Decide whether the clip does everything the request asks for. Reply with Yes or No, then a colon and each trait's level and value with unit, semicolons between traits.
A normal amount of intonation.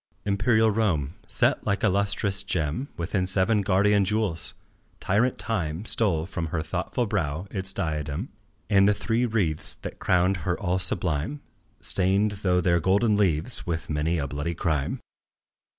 Yes: average, 4.0 semitones